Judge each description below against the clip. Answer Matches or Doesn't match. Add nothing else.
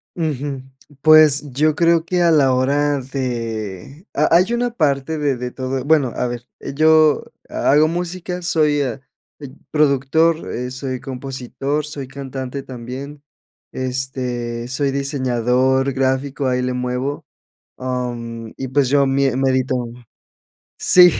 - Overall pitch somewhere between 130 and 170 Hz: Matches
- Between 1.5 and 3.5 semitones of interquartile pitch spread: Matches